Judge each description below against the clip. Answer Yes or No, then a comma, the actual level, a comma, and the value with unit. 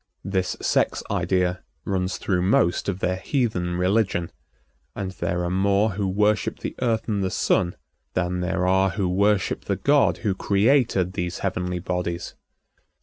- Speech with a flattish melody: Yes, narrow, 2.0 semitones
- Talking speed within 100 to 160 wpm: Yes, average, 150 wpm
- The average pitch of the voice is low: Yes, very low, 95 Hz